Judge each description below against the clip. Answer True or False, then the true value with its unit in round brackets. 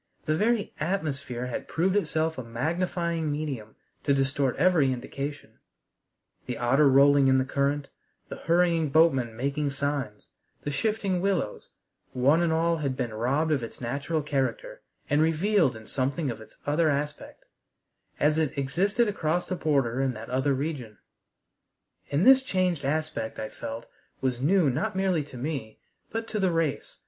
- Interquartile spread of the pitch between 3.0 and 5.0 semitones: True (4.2 semitones)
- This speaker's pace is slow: False (155 wpm)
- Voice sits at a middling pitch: True (145 Hz)